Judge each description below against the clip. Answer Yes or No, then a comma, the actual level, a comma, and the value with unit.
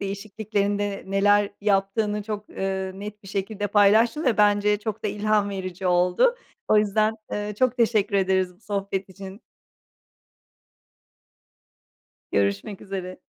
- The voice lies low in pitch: No, high, 205 Hz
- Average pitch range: No, narrow, 1.6 semitones